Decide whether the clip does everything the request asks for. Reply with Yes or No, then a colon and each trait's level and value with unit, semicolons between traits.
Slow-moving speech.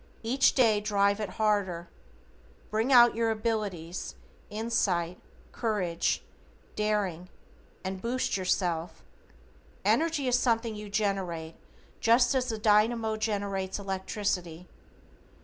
Yes: slow, 100 wpm